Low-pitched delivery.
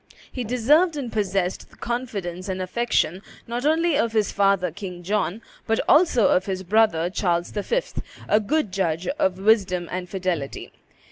No: high, 200 Hz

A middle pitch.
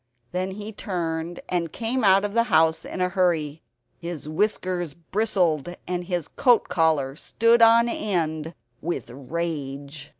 Yes: medium, 175 Hz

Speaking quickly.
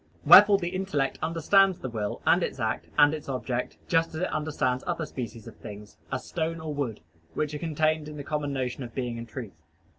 Yes: fast, 210 wpm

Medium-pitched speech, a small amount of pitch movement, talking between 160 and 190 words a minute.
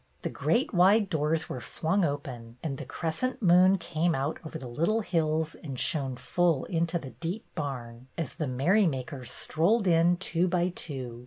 No: medium, 160 Hz; average, 4.8 semitones; average, 170 wpm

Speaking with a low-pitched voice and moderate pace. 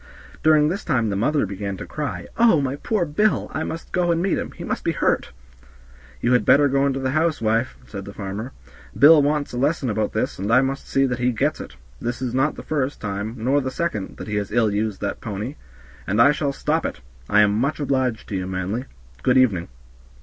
No: low, 130 Hz; fast, 230 wpm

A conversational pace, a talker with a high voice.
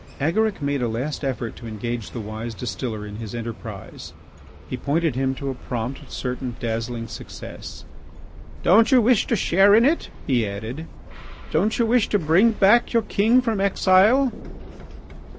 No: average, 160 wpm; medium, 140 Hz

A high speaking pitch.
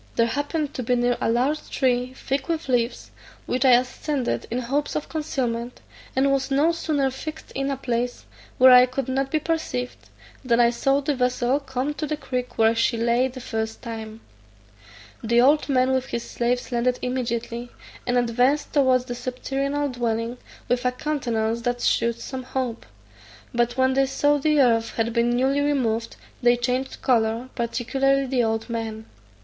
Yes: very high, 250 Hz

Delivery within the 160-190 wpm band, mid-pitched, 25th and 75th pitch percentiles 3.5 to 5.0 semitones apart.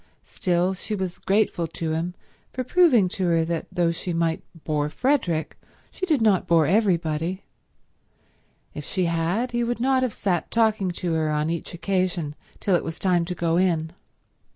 Yes: average, 175 wpm; medium, 180 Hz; average, 4.1 semitones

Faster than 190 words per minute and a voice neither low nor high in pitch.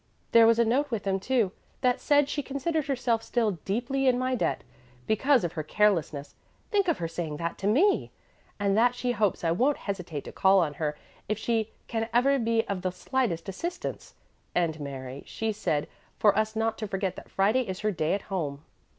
No: average, 200 wpm; high, 215 Hz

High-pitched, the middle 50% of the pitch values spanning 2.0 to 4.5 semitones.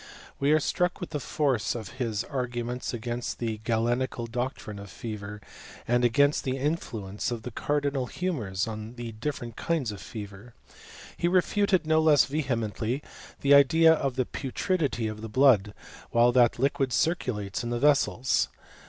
No: low, 125 Hz; average, 4.2 semitones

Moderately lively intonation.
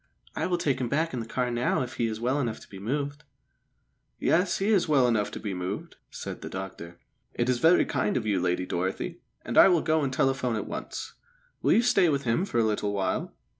No: wide, 5.8 semitones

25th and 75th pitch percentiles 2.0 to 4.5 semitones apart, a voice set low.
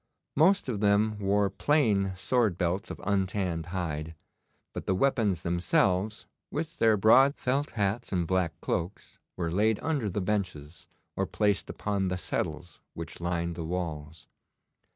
Yes: average, 3.7 semitones; very low, 95 Hz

